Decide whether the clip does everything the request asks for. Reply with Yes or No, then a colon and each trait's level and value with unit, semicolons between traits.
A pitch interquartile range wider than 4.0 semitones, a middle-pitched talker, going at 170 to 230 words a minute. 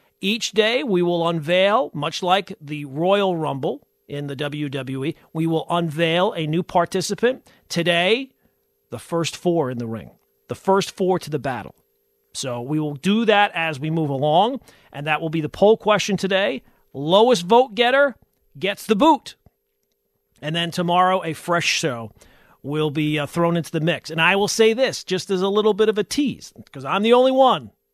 Yes: average, 5.2 semitones; medium, 175 Hz; average, 185 wpm